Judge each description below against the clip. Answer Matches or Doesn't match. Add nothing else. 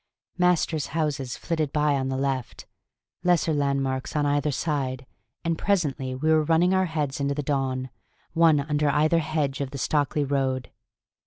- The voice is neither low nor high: Matches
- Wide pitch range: Doesn't match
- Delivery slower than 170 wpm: Matches